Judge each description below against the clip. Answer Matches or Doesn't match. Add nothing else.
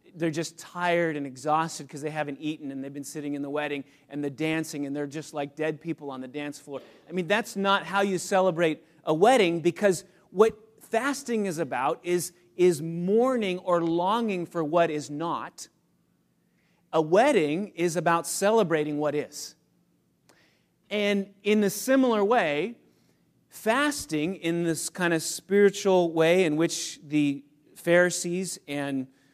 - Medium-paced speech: Matches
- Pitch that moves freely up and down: Doesn't match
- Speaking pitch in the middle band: Matches